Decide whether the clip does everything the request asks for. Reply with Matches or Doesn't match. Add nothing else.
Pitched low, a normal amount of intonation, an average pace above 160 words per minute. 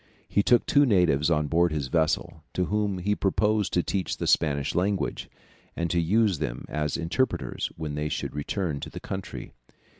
Matches